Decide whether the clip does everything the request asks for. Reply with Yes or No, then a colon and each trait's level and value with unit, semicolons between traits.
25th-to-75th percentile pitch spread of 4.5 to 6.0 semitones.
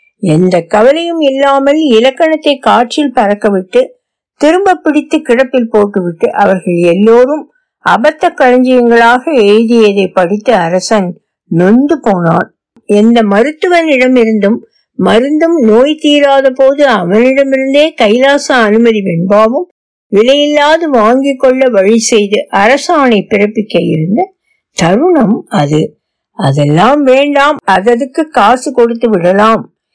Yes: wide, 5.6 semitones